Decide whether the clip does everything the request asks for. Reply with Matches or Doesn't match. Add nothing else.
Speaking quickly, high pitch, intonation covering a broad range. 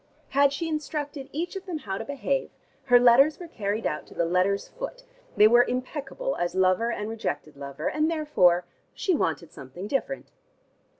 Doesn't match